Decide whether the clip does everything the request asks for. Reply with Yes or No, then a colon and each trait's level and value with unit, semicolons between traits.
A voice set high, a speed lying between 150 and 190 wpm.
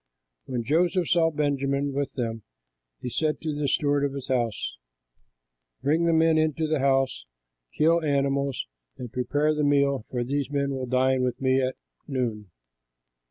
No: medium, 140 Hz; average, 160 wpm